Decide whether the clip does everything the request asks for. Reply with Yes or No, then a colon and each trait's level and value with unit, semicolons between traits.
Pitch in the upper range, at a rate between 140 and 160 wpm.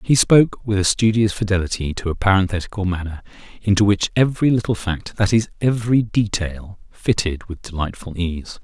No: low, 100 Hz; average, 145 wpm